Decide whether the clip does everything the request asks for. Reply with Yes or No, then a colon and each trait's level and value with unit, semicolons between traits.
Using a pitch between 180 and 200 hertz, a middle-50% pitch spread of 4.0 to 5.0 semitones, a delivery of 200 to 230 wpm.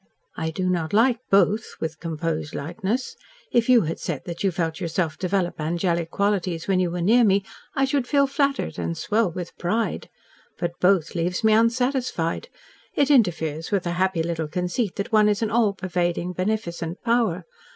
No: medium, 185 Hz; average, 4.7 semitones; average, 175 wpm